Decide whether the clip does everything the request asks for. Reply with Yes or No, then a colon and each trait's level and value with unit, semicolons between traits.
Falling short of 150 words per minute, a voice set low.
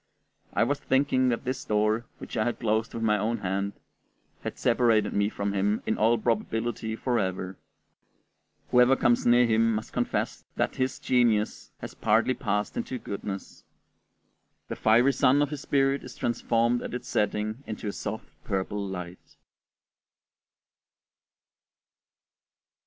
Yes: average, 140 wpm; low, 115 Hz